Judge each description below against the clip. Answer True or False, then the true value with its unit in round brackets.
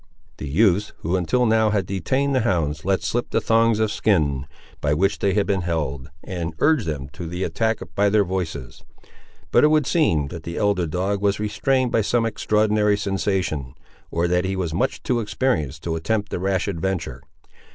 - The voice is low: True (95 Hz)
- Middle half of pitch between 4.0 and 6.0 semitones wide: True (4.7 semitones)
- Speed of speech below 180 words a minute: False (190 wpm)